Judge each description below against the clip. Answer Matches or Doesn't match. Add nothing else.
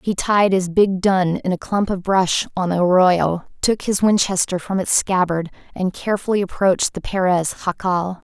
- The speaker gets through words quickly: Doesn't match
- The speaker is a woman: Matches